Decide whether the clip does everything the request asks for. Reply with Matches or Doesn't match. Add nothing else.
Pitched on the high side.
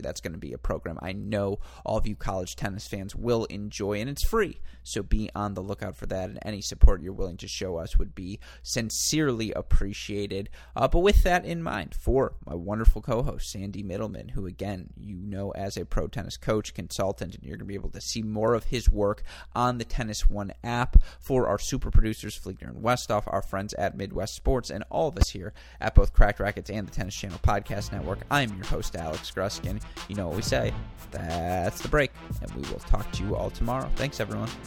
Doesn't match